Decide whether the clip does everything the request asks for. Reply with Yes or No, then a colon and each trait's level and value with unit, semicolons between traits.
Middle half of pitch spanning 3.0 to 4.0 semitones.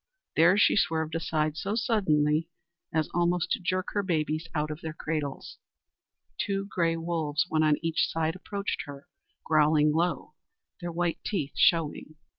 No: narrow, 2.4 semitones